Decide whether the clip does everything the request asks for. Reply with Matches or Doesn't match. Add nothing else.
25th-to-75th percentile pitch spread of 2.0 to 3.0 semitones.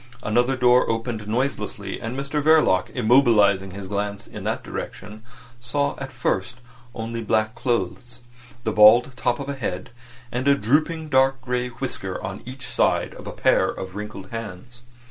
Doesn't match